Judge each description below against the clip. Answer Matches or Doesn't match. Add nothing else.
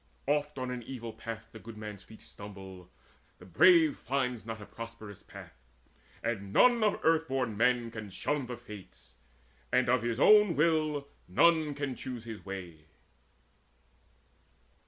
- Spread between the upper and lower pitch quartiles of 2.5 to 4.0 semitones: Doesn't match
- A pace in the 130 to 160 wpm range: Matches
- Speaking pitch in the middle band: Doesn't match